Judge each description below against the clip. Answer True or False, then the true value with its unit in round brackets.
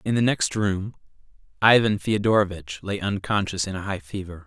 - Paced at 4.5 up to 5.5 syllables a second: True (5.2 syllables/s)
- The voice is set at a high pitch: False (100 Hz)